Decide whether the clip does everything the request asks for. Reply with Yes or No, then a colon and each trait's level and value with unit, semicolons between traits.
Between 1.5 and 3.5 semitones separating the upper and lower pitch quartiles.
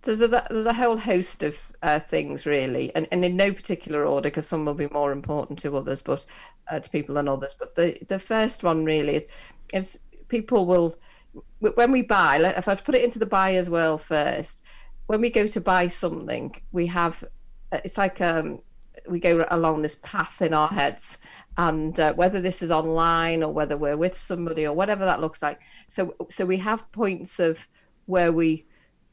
No: average, 4.1 semitones